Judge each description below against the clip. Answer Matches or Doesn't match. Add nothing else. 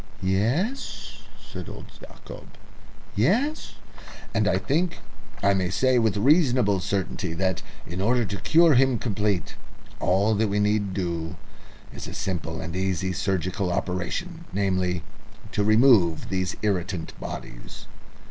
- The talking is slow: Matches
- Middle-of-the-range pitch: Doesn't match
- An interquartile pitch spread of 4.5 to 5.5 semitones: Matches